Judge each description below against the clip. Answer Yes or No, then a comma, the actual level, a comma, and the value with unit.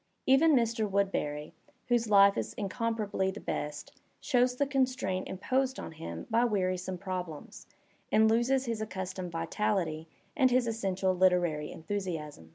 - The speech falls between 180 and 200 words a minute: No, slow, 135 wpm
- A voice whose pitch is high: Yes, high, 200 Hz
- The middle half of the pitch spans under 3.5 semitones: No, average, 4.6 semitones